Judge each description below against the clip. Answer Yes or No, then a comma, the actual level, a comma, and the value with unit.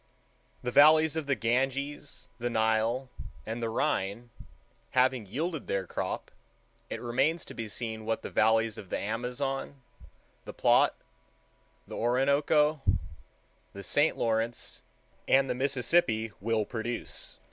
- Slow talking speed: Yes, slow, 125 wpm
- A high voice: No, low, 120 Hz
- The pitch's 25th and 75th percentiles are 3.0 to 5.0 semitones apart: Yes, average, 3.7 semitones